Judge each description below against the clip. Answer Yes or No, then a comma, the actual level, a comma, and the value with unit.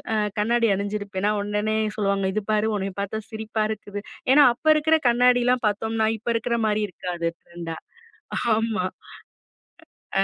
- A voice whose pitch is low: No, high, 215 Hz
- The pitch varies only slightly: Yes, narrow, 2.3 semitones